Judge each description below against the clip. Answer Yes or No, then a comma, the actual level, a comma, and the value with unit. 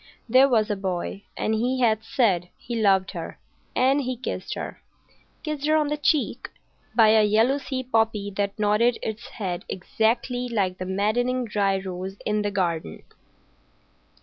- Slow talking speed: No, average, 150 wpm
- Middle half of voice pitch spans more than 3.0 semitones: Yes, average, 4.0 semitones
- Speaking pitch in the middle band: No, high, 220 Hz